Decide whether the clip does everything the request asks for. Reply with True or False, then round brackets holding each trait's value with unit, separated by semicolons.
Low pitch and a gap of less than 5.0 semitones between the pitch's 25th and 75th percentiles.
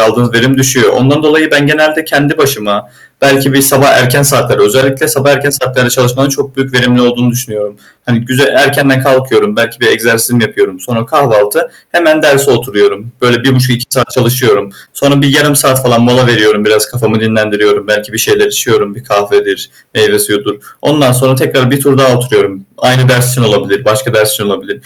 True (130 Hz; 3.3 semitones)